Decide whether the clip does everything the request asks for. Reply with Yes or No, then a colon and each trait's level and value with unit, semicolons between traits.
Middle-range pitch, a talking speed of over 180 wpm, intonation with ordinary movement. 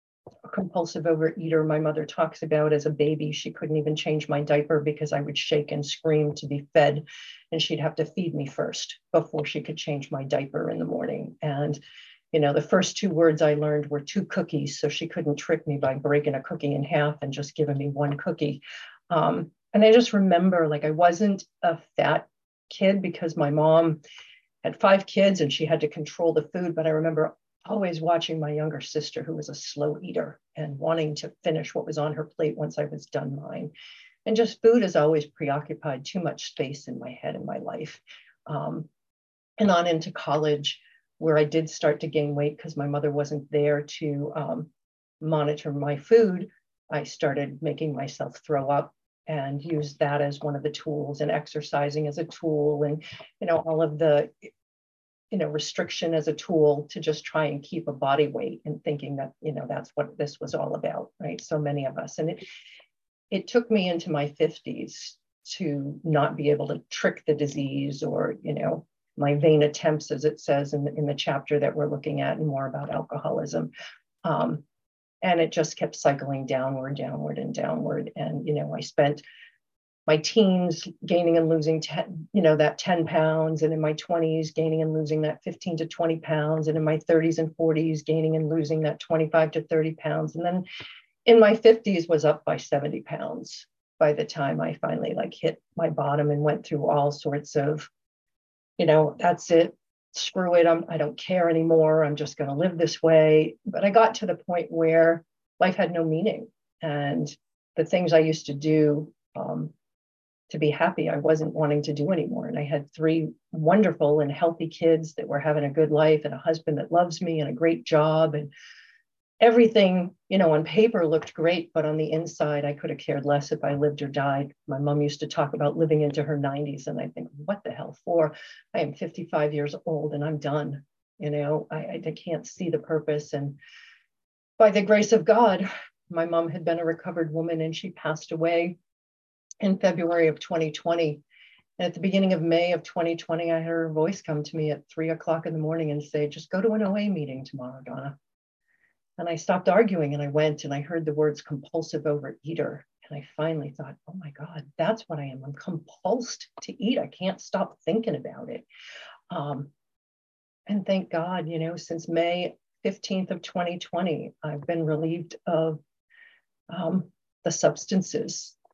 No: medium, 155 Hz; average, 200 wpm; narrow, 2.1 semitones